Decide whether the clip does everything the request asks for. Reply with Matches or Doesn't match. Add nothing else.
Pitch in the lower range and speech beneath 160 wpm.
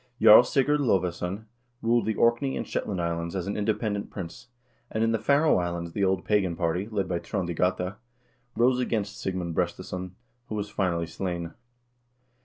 Doesn't match